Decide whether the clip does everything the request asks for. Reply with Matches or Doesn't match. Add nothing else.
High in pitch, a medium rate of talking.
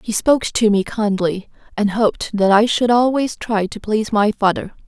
Matches